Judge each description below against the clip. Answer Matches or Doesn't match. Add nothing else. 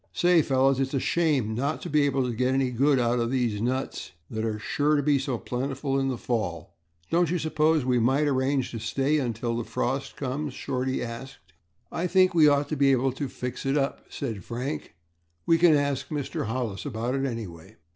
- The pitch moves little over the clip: Doesn't match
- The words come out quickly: Matches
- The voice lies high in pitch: Doesn't match